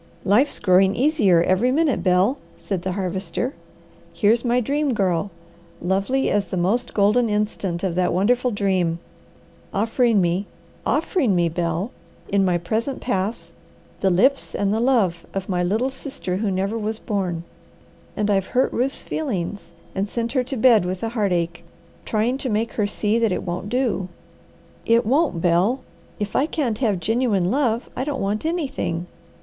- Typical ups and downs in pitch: Yes, average, 4.9 semitones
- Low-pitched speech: No, high, 210 Hz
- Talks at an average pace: Yes, average, 165 wpm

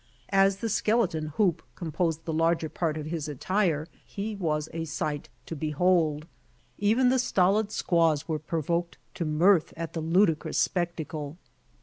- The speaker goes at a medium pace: Yes, average, 145 wpm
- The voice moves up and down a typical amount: Yes, average, 3.6 semitones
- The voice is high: No, medium, 165 Hz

